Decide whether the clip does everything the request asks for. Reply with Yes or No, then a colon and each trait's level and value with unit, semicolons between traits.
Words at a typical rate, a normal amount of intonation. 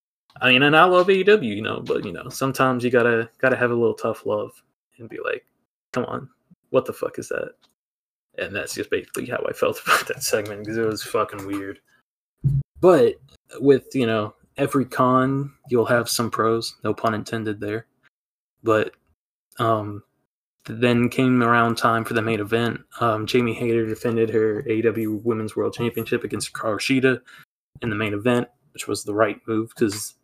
Yes: average, 180 wpm; average, 3.5 semitones